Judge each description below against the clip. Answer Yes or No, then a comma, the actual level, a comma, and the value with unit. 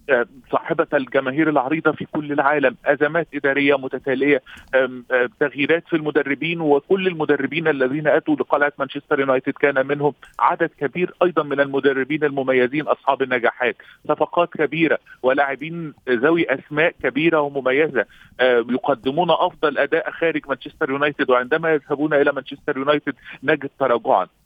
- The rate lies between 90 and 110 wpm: No, average, 125 wpm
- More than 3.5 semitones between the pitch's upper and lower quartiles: No, narrow, 2.4 semitones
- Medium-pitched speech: Yes, medium, 145 Hz